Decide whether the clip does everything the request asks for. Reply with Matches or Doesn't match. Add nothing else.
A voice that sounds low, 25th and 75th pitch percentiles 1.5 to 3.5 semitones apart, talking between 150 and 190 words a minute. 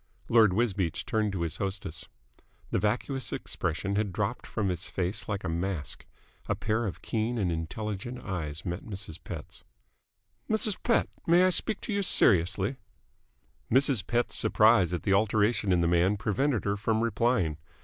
Doesn't match